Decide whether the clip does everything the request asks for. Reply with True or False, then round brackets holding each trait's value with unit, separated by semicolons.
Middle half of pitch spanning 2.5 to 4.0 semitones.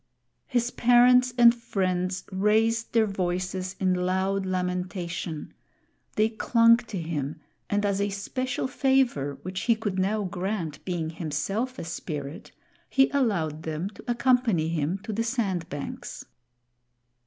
False (4.7 semitones)